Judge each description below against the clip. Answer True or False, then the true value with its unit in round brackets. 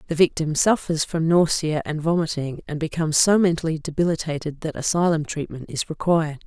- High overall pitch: False (160 Hz)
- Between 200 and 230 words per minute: False (160 wpm)